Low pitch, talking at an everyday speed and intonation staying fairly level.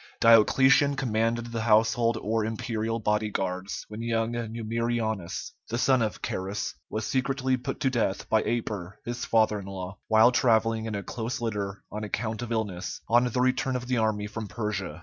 Yes: low, 115 Hz; average, 175 wpm; narrow, 2.0 semitones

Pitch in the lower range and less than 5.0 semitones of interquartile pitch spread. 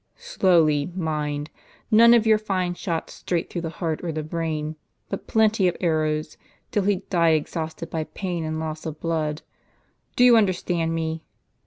No: medium, 165 Hz; average, 3.1 semitones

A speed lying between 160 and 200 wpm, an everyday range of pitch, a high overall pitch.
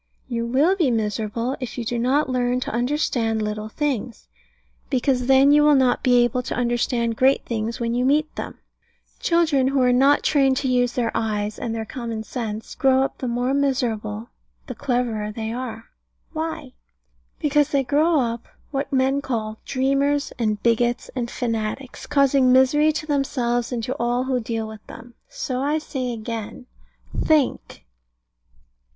Yes: average, 165 wpm; average, 3.0 semitones; very high, 250 Hz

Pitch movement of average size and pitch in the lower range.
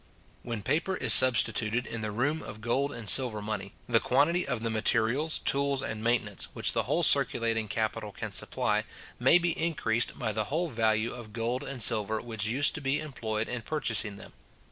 Yes: average, 4.0 semitones; low, 115 Hz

